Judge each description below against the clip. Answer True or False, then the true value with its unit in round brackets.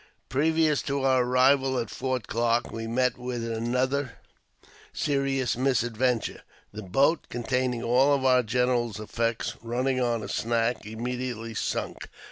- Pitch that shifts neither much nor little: False (2.2 semitones)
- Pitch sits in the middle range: False (125 Hz)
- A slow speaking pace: True (125 wpm)